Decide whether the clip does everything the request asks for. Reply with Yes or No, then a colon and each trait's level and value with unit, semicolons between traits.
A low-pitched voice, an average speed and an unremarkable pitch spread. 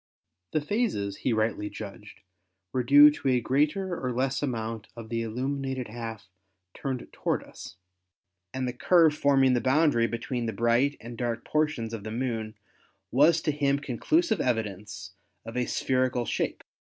Yes: low, 125 Hz; average, 155 wpm; average, 3.9 semitones